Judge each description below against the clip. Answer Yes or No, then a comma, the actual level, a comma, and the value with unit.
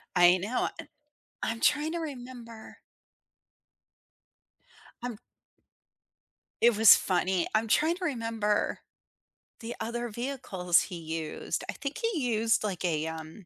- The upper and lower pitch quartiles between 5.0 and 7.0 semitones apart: Yes, wide, 5.5 semitones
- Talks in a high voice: Yes, high, 225 Hz